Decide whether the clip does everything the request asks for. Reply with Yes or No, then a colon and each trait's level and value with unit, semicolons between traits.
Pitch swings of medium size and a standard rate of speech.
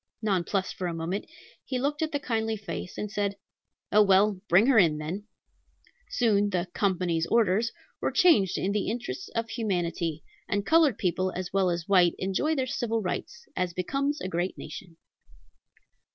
Yes: average, 4.1 semitones; average, 165 wpm